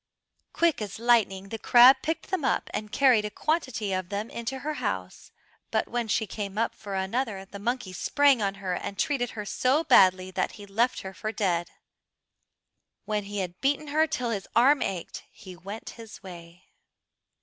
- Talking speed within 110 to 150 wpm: No, average, 185 wpm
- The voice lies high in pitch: Yes, high, 210 Hz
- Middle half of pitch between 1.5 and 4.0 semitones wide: No, average, 4.6 semitones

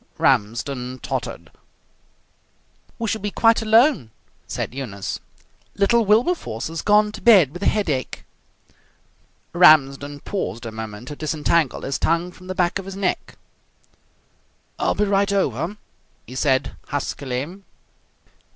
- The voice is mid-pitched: Yes, medium, 165 Hz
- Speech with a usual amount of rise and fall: No, wide, 7.4 semitones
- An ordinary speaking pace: No, slow, 125 wpm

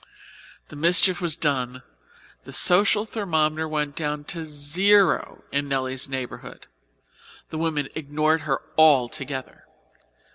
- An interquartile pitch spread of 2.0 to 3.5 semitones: Yes, average, 2.9 semitones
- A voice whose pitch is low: No, medium, 155 Hz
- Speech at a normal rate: No, slow, 110 wpm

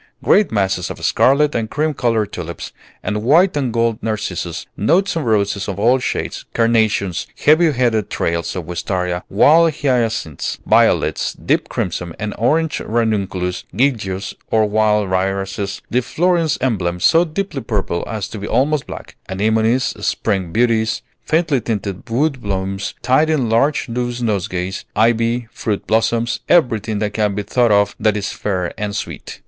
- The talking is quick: No, average, 150 wpm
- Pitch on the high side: No, low, 110 Hz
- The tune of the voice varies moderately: Yes, average, 4.2 semitones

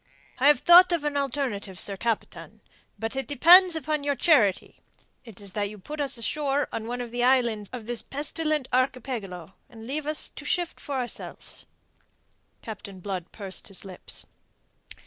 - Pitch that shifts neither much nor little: No, wide, 5.7 semitones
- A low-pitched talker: No, very high, 250 Hz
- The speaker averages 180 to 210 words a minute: No, average, 165 wpm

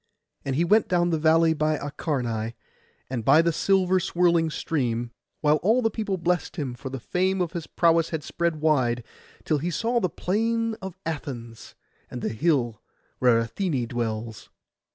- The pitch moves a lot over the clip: Yes, wide, 6.3 semitones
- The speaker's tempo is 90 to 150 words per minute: No, average, 170 wpm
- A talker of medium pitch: Yes, medium, 160 Hz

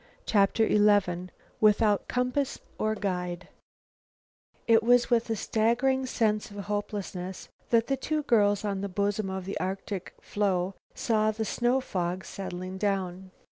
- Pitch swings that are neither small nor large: Yes, average, 3.0 semitones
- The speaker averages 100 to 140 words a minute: Yes, slow, 135 wpm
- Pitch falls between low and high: No, high, 205 Hz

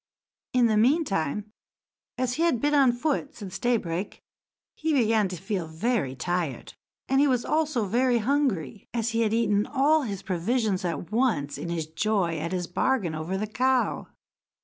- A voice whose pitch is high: Yes, high, 220 Hz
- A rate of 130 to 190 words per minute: Yes, average, 170 wpm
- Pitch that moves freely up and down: Yes, wide, 6.2 semitones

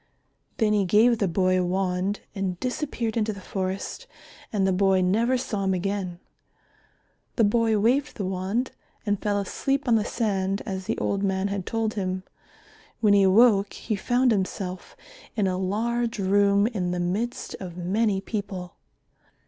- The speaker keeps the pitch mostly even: No, average, 3.0 semitones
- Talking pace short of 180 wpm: Yes, average, 165 wpm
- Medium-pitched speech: No, high, 200 Hz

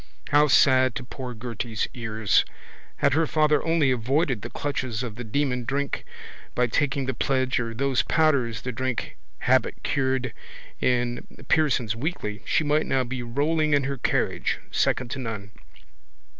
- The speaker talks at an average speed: Yes, average, 155 wpm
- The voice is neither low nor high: No, low, 130 Hz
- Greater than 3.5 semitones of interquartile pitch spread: No, average, 3.2 semitones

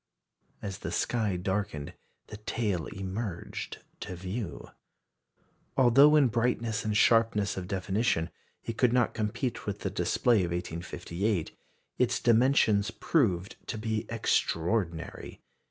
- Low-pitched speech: Yes, low, 105 Hz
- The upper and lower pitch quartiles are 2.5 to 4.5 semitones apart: Yes, average, 4.0 semitones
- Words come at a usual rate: No, slow, 120 wpm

